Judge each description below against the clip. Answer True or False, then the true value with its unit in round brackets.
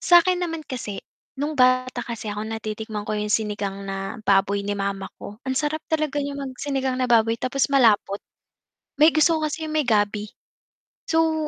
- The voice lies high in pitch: True (250 Hz)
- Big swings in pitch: True (6.2 semitones)